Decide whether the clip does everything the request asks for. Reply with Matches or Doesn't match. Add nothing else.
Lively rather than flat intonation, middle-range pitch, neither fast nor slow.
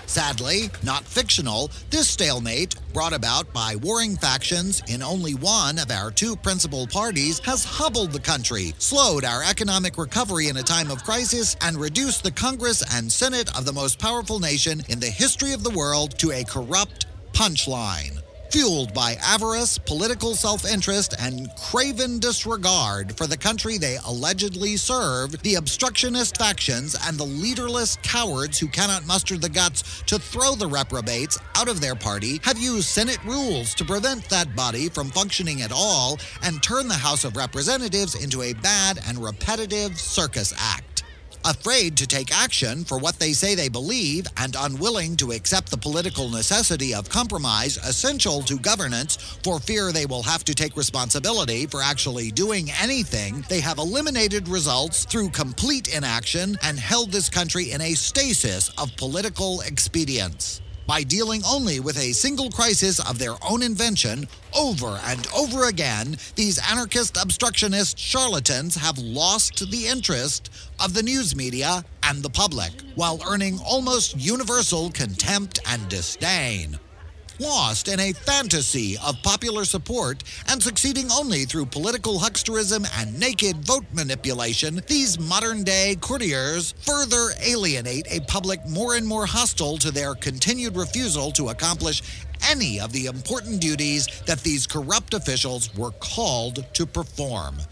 Matches